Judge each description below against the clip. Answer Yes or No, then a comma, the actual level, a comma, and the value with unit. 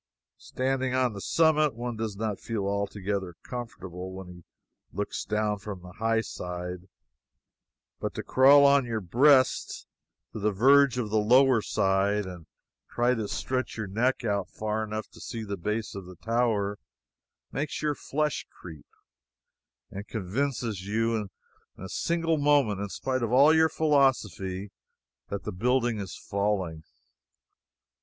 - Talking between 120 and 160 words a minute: Yes, average, 150 wpm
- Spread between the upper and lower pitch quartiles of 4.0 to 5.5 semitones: Yes, average, 4.7 semitones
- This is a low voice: Yes, low, 110 Hz